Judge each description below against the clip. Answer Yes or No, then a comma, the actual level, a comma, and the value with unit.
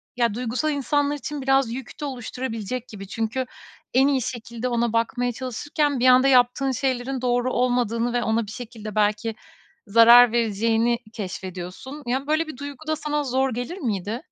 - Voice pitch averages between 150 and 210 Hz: No, high, 245 Hz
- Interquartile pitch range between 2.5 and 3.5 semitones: Yes, average, 2.8 semitones